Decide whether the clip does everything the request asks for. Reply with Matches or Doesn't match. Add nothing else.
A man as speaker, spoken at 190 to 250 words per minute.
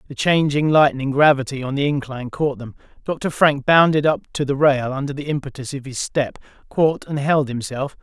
Matches